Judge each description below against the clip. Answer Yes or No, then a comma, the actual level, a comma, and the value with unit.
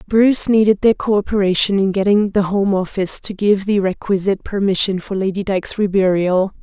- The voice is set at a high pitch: Yes, high, 195 Hz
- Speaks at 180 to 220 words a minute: No, average, 165 wpm